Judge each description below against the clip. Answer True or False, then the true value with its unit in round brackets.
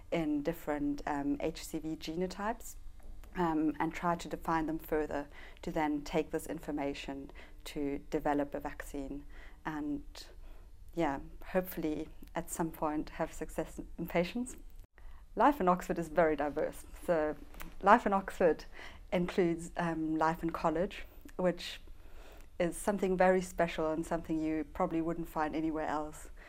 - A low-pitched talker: False (160 Hz)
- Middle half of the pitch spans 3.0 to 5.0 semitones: False (2.4 semitones)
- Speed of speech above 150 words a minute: False (135 wpm)